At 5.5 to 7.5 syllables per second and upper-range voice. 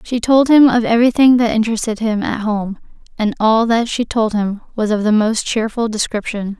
No: 5.2 syllables/s; high, 225 Hz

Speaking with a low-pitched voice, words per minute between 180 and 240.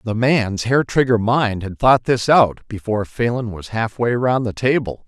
Yes: low, 115 Hz; average, 200 wpm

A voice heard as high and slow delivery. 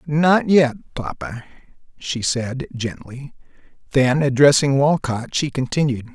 No: low, 135 Hz; slow, 105 wpm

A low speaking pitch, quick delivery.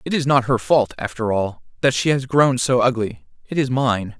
Yes: low, 125 Hz; fast, 230 wpm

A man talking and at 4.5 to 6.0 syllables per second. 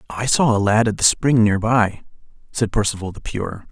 Yes: male; 5.0 syllables/s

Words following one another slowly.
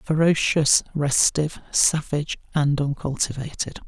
Yes: slow, 75 wpm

